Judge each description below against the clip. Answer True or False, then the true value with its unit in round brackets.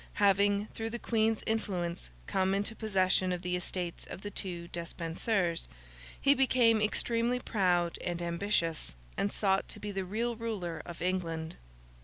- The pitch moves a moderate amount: True (4.0 semitones)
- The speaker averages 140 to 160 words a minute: True (150 wpm)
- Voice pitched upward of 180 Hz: True (190 Hz)